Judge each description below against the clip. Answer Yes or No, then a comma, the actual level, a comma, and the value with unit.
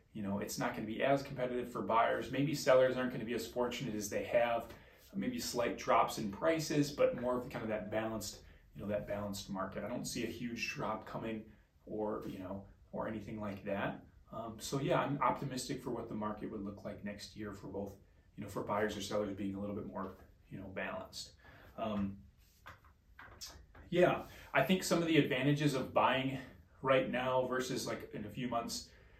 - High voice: No, low, 110 Hz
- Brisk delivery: Yes, fast, 210 wpm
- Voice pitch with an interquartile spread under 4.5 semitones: Yes, average, 4.0 semitones